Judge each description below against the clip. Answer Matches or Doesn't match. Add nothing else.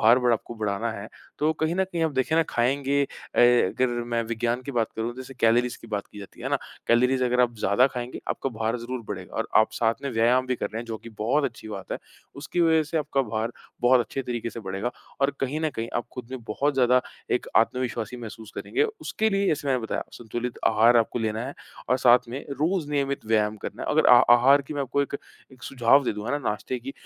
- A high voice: Doesn't match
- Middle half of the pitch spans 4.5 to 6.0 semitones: Doesn't match